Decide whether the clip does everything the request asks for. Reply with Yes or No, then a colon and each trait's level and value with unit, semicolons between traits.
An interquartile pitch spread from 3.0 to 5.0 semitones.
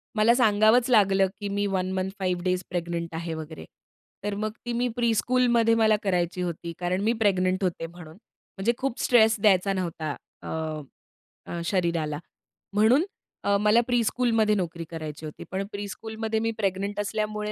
Yes: average, 3.8 semitones